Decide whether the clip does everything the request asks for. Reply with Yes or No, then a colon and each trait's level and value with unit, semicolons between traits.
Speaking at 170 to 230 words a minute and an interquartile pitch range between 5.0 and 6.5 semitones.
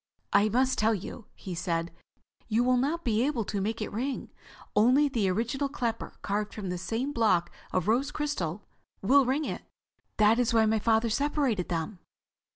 No: average, 175 wpm; average, 4.3 semitones